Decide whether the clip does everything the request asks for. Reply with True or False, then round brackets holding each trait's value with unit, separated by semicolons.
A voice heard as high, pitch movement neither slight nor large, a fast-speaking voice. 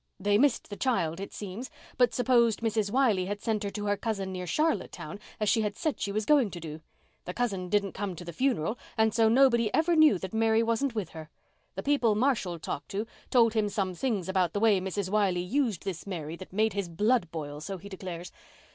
True (205 Hz; 3.8 semitones; 220 wpm)